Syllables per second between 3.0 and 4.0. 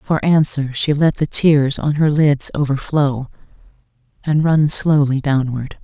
Yes: 3.9 syllables/s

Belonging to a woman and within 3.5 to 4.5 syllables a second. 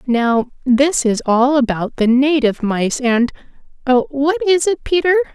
Yes: female; 4.0 syllables/s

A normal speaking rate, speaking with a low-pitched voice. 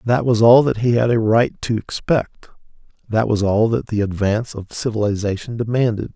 Yes: average, 185 wpm; low, 115 Hz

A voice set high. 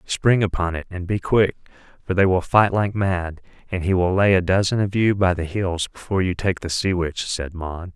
No: very low, 95 Hz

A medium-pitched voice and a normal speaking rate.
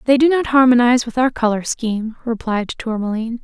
No: high, 240 Hz; average, 175 wpm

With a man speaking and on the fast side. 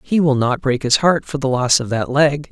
Yes: male; fast, 285 wpm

